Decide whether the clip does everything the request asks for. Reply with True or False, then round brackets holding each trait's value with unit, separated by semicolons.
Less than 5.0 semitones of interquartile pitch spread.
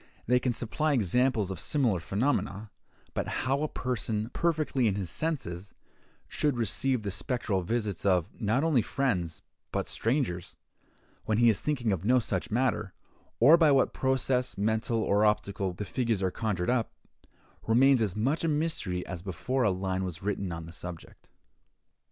False (5.3 semitones)